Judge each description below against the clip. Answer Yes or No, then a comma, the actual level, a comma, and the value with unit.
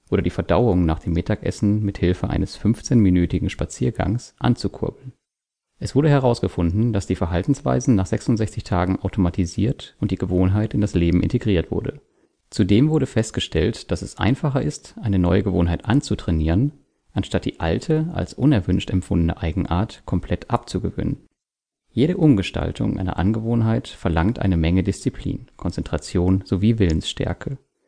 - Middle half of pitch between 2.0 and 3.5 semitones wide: No, average, 4.7 semitones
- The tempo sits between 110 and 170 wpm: Yes, average, 130 wpm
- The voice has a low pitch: Yes, low, 100 Hz